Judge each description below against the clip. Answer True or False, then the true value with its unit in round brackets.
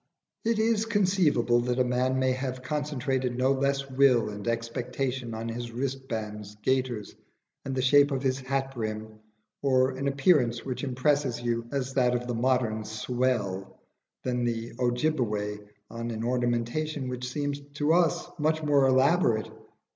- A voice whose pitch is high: False (130 Hz)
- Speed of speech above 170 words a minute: False (150 wpm)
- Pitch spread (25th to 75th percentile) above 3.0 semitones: False (2.7 semitones)